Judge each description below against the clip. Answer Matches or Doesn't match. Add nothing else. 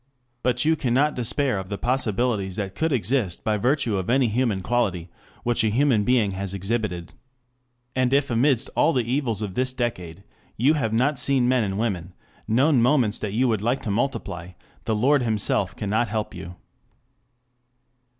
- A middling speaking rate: Matches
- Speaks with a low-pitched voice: Matches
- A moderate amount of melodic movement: Matches